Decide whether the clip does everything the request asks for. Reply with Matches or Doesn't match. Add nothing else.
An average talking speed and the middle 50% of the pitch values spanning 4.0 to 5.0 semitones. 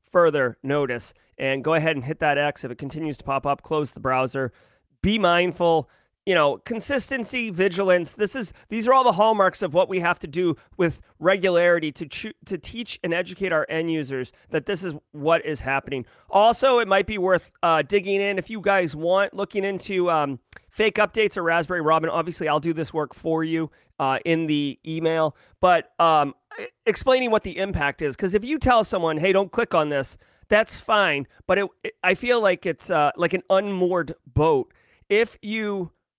Matches